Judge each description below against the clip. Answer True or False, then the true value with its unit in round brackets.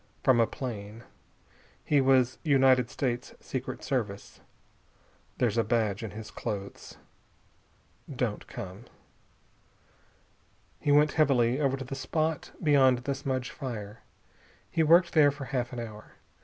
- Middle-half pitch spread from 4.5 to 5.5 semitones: False (3.4 semitones)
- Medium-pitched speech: False (130 Hz)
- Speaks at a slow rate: True (130 wpm)